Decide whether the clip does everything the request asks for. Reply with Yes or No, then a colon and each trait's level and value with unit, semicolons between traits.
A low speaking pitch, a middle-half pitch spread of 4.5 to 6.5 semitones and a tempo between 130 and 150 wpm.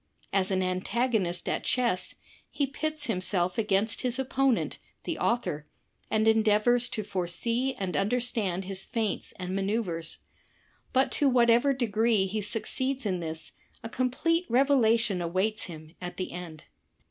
No: high, 220 Hz; average, 4.9 semitones; average, 140 wpm